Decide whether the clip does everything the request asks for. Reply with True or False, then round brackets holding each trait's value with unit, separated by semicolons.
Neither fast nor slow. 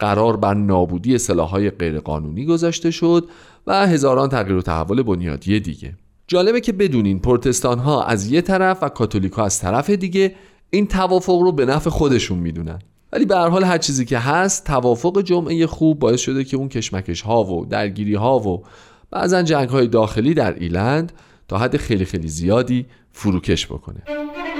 False (170 wpm)